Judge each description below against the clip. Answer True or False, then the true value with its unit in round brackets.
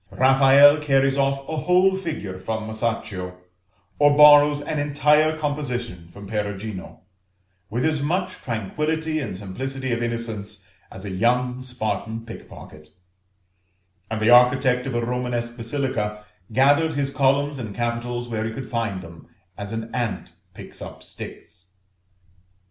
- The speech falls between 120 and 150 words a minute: True (135 wpm)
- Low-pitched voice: True (125 Hz)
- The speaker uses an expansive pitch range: False (4.6 semitones)